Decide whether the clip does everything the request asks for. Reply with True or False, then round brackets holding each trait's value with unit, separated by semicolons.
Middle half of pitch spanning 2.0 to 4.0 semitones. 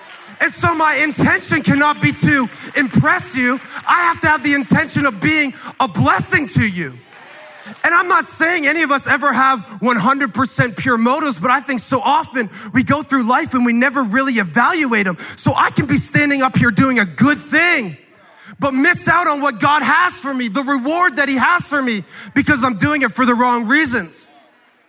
True (3.4 semitones)